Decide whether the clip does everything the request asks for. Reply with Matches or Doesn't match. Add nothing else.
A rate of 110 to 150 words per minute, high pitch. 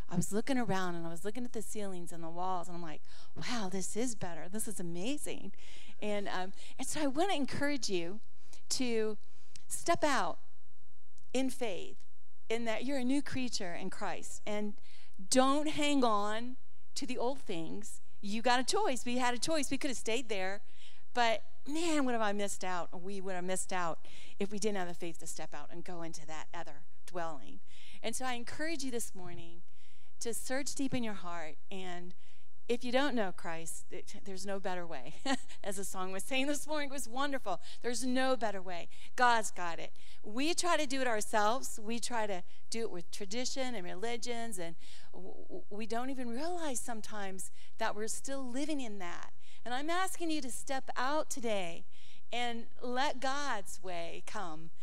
Doesn't match